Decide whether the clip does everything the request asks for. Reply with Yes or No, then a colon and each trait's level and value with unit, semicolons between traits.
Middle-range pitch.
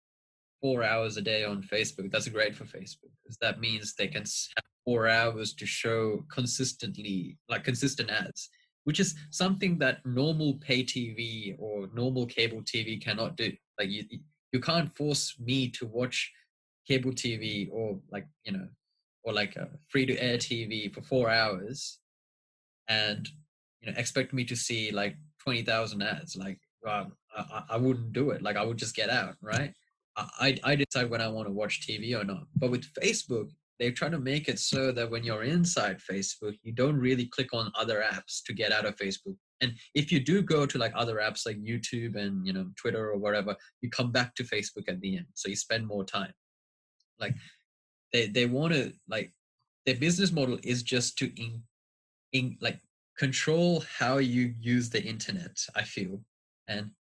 No: low, 120 Hz